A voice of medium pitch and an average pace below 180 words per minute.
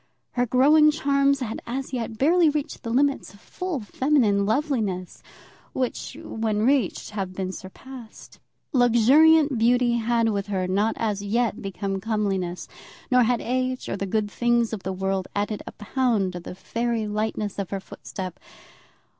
No: high, 225 Hz; average, 155 wpm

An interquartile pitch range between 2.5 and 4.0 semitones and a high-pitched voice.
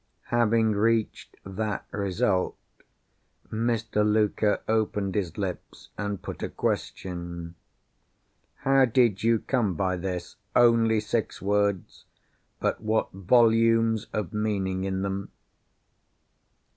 No: average, 2.9 semitones; low, 105 Hz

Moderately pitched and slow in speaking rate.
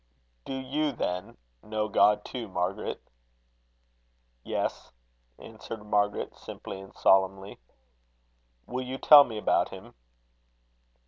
No: low, 105 Hz; slow, 105 wpm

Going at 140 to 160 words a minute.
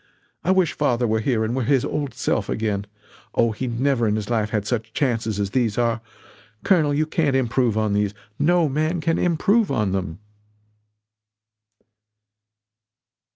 Yes: average, 155 wpm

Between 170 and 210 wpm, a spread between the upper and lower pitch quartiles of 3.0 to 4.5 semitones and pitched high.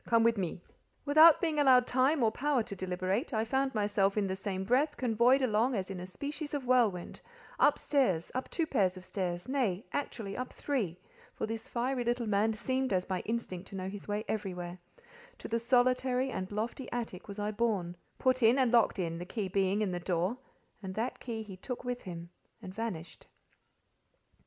No: average, 195 wpm; average, 5.1 semitones; high, 220 Hz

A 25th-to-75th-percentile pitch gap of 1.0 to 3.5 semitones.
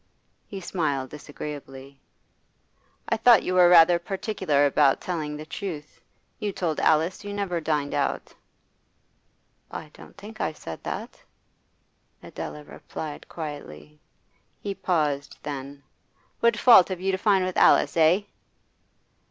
No: average, 4.6 semitones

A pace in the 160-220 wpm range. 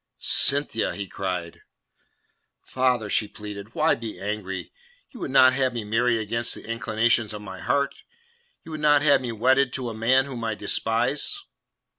Yes: average, 165 wpm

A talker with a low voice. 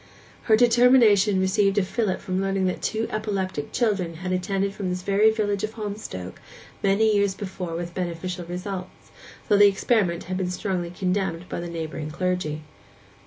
No: high, 190 Hz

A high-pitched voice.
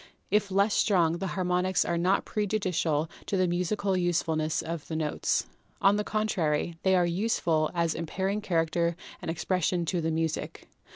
No: medium, 175 Hz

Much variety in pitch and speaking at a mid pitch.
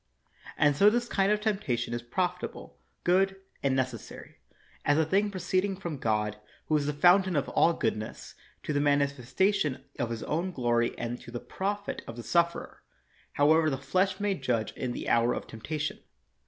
Yes: wide, 7.4 semitones; medium, 150 Hz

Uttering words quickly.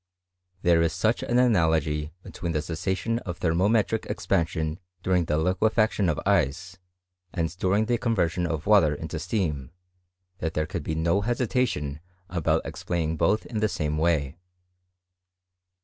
No: average, 140 wpm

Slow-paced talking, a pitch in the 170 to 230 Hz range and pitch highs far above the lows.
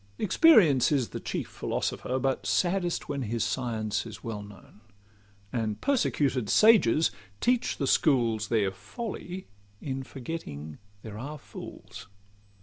No: slow, 125 wpm; low, 130 Hz; wide, 7.0 semitones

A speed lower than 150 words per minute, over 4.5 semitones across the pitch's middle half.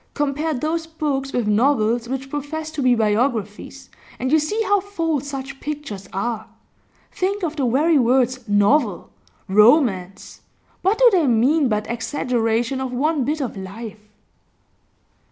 Yes: average, 140 wpm; average, 5.2 semitones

